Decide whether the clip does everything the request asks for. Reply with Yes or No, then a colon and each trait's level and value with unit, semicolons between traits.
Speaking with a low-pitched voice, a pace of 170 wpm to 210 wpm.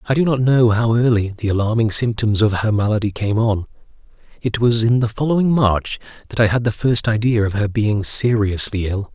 Yes: low, 110 Hz; fast, 205 wpm